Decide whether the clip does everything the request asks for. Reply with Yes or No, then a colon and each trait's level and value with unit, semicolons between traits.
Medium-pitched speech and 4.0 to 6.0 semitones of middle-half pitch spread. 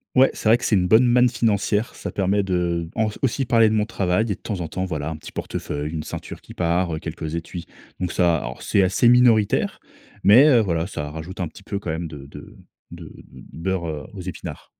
No: very low, 95 Hz; average, 4.8 semitones